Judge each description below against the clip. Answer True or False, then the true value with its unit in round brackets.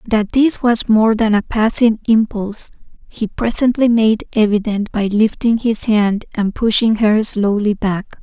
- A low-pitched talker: False (220 Hz)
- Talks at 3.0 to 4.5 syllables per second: True (4.2 syllables/s)